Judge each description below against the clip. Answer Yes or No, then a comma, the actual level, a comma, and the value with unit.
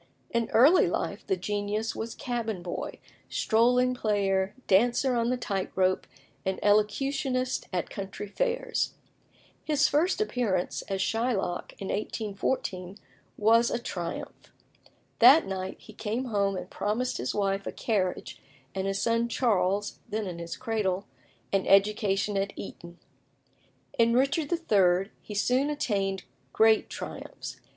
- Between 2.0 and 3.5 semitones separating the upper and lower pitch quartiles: No, average, 4.0 semitones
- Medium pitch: No, high, 210 Hz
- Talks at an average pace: No, slow, 130 wpm